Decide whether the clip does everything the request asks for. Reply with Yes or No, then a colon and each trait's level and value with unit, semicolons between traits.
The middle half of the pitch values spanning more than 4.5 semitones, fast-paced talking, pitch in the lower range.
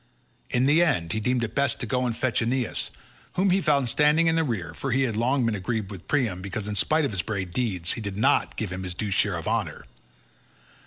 Yes: wide, 5.5 semitones; fast, 245 wpm; low, 115 Hz